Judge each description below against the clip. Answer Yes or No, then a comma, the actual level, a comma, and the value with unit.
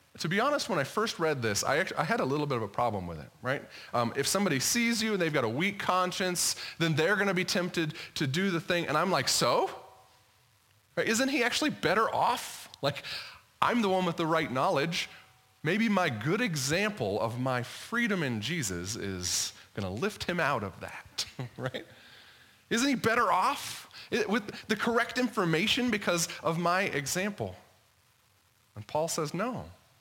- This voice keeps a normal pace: Yes, average, 185 wpm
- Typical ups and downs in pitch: No, wide, 8.8 semitones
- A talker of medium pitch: Yes, medium, 160 Hz